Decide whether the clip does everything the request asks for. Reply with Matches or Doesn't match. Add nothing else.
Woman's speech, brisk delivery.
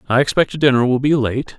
Doesn't match